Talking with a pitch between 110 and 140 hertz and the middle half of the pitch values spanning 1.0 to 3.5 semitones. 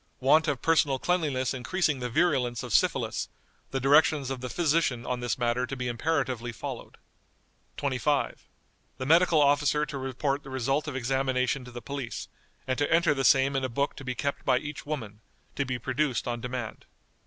Yes: low, 135 Hz; average, 2.7 semitones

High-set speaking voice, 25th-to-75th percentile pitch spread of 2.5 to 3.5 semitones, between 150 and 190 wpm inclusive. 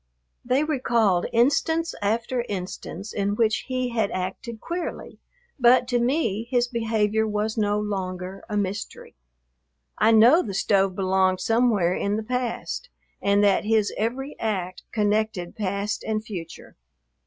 No: high, 215 Hz; average, 3.2 semitones; slow, 135 wpm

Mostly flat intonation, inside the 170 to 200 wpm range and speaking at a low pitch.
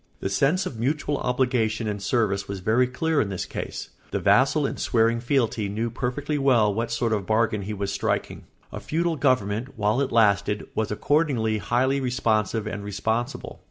No: average, 3.8 semitones; average, 180 wpm; low, 115 Hz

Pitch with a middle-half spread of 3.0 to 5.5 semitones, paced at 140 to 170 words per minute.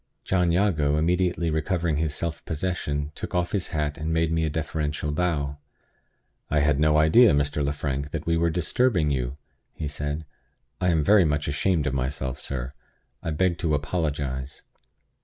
No: narrow, 2.6 semitones; average, 165 wpm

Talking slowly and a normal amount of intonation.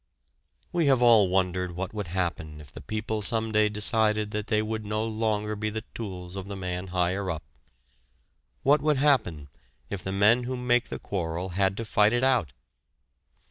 No: average, 180 wpm; average, 3.4 semitones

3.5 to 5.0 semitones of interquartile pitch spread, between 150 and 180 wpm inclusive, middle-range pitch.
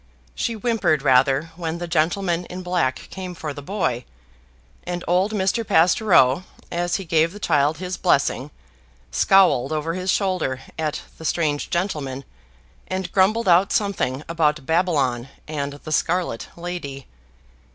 No: average, 4.1 semitones; average, 140 wpm; medium, 170 Hz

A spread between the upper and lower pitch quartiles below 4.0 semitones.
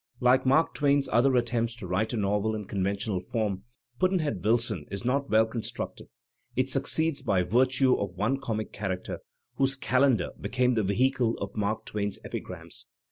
No: average, 4.4 semitones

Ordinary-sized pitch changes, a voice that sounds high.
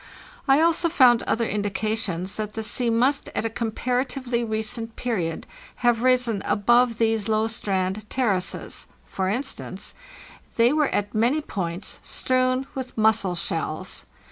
Yes: average, 3.5 semitones; high, 225 Hz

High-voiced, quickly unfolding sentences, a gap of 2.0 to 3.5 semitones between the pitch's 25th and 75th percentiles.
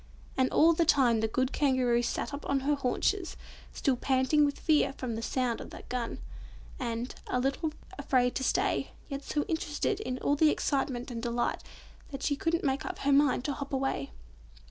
No: very high, 270 Hz; average, 190 wpm; average, 2.9 semitones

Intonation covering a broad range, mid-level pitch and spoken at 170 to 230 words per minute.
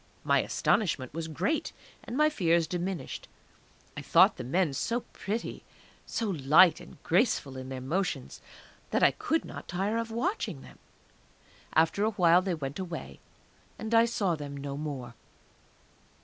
No: wide, 6.9 semitones; medium, 175 Hz; average, 150 wpm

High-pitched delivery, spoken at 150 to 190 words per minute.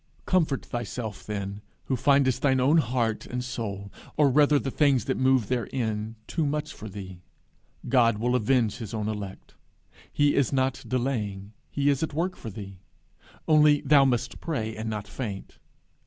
No: low, 125 Hz; average, 165 wpm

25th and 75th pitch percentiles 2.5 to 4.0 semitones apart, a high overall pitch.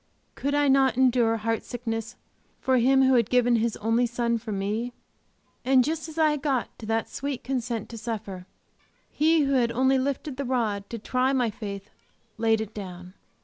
Yes: average, 3.0 semitones; high, 240 Hz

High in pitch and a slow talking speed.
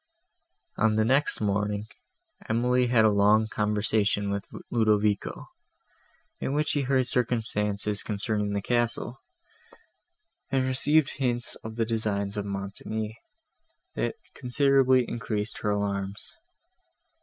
No: low, 110 Hz; slow, 110 wpm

